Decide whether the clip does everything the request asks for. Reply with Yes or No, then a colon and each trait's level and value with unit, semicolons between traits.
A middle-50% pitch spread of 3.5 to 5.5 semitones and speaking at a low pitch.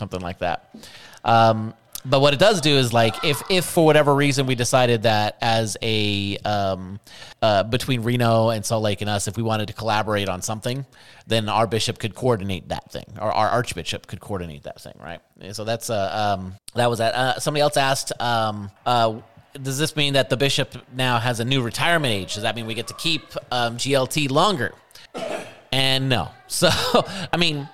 Yes: average, 4.1 semitones; low, 115 Hz